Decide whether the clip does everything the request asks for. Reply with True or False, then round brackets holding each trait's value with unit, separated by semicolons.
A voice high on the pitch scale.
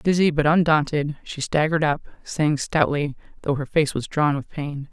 False (150 Hz)